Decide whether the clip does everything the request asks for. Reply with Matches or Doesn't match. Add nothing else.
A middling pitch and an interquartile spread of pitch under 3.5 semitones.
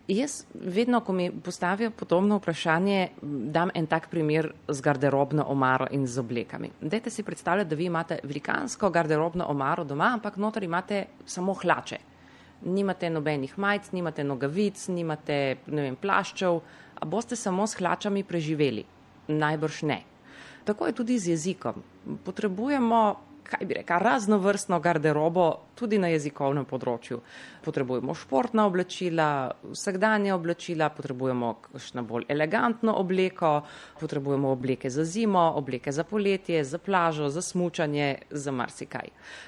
Doesn't match